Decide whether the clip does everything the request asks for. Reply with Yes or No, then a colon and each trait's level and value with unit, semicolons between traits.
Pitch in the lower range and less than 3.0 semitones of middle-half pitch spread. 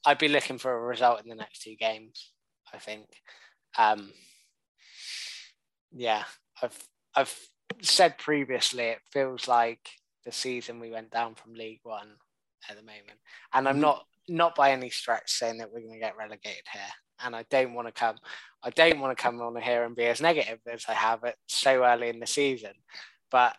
Yes: low, 120 Hz; narrow, 2.5 semitones